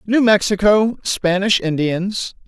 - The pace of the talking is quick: No, slow, 95 wpm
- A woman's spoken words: No, male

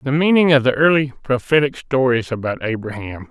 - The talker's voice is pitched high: No, low, 130 Hz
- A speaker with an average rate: Yes, average, 165 wpm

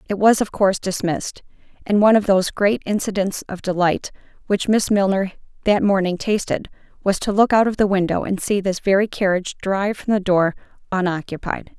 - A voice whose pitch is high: Yes, high, 195 Hz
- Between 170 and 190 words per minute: Yes, average, 180 wpm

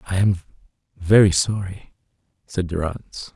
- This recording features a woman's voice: No, male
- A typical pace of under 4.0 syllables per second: Yes, 3.8 syllables/s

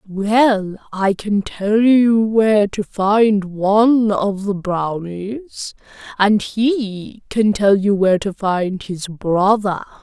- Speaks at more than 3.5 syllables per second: No, 3.0 syllables/s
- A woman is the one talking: Yes, female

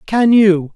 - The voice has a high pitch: Yes, high, 200 Hz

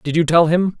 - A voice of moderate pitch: Yes, medium, 165 Hz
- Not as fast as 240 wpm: No, fast, 300 wpm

